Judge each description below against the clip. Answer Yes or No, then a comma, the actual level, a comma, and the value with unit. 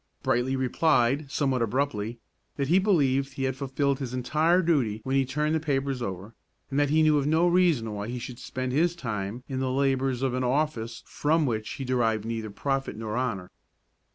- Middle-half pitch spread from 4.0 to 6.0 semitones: No, average, 3.6 semitones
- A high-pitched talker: No, low, 130 Hz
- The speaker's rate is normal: Yes, average, 195 wpm